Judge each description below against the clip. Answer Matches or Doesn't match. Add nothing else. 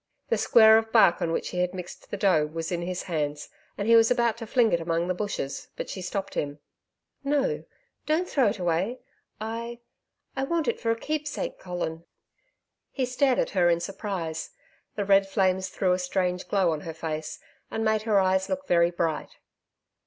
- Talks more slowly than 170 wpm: Doesn't match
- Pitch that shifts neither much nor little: Matches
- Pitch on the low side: Doesn't match